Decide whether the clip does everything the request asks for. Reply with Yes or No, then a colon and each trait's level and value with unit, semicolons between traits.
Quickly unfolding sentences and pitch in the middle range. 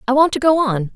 No: fast, 315 wpm; very high, 265 Hz